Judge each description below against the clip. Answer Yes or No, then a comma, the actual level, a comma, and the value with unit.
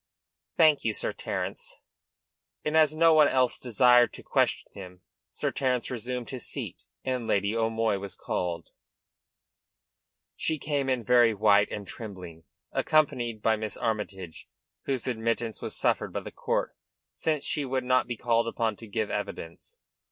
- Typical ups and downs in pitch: Yes, average, 3.7 semitones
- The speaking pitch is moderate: No, low, 115 Hz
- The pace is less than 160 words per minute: Yes, average, 150 wpm